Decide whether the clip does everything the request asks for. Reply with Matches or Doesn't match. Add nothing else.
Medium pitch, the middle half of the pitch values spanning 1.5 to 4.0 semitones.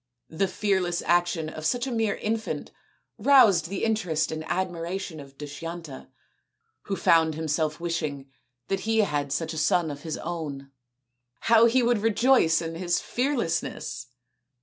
Doesn't match